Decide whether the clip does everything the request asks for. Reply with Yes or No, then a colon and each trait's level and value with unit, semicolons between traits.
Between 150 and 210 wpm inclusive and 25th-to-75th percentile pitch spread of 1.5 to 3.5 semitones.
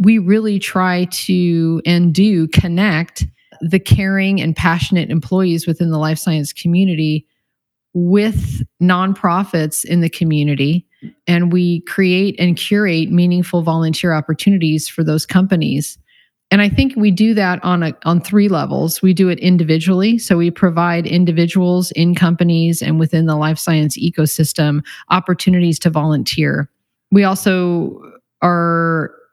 No: slow, 135 wpm; narrow, 2.5 semitones